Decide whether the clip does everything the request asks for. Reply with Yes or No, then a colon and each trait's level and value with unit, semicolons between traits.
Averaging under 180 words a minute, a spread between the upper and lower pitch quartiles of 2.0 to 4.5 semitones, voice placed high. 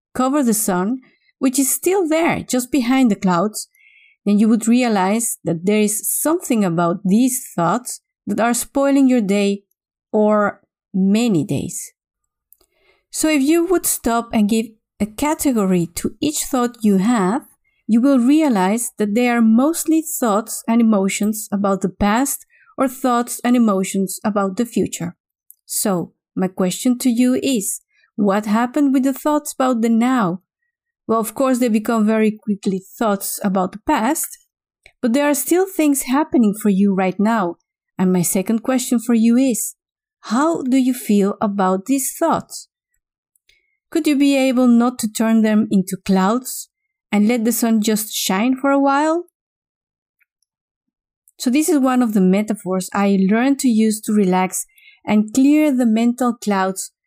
No: average, 160 wpm; average, 5.1 semitones; high, 235 Hz